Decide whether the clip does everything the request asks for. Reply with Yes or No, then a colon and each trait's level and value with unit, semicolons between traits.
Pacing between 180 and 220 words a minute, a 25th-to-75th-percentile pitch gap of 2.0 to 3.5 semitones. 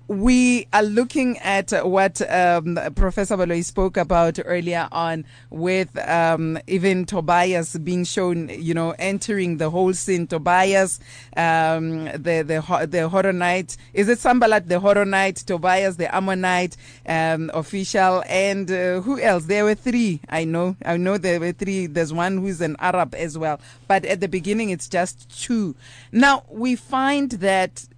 No: average, 155 wpm; average, 2.8 semitones